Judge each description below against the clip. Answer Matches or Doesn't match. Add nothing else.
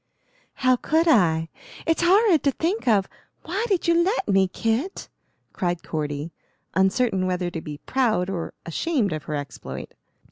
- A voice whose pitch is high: Matches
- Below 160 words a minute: Matches